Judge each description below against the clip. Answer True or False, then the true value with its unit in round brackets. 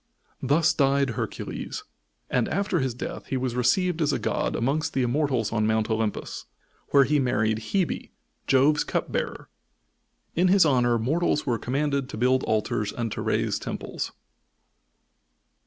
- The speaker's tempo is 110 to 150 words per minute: True (145 wpm)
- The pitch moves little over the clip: False (4.3 semitones)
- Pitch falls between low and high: False (130 Hz)